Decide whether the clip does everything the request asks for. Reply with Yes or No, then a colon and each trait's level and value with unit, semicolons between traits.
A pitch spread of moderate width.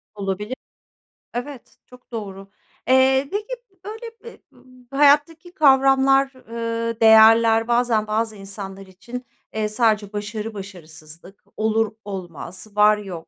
Yes: average, 4.5 semitones